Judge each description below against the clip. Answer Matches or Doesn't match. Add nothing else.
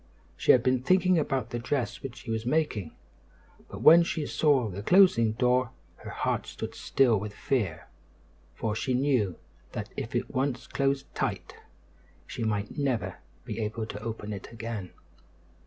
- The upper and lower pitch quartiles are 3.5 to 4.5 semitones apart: Matches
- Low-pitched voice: Matches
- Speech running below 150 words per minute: Doesn't match